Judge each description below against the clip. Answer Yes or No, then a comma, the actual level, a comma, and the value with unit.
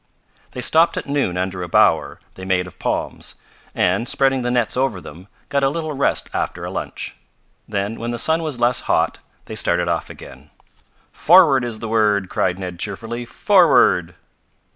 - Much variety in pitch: Yes, wide, 6.3 semitones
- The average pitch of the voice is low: Yes, low, 115 Hz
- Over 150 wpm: Yes, average, 175 wpm